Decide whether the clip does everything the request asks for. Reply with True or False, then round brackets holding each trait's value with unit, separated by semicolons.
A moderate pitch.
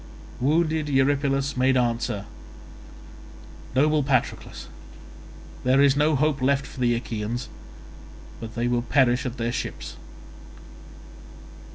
False (130 Hz)